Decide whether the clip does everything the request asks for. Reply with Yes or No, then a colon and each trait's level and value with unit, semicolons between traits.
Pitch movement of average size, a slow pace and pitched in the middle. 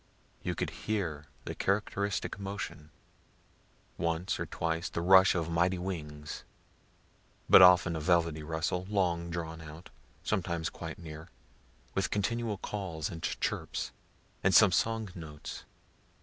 No: average, 3.0 semitones; slow, 125 wpm; very low, 85 Hz